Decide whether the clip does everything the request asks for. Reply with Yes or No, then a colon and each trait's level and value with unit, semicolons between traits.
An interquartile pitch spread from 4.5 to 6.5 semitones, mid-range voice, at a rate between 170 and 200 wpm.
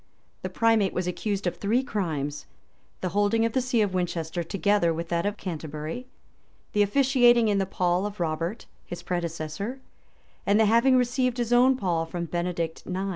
No: average, 5.0 semitones; high, 195 Hz; average, 175 wpm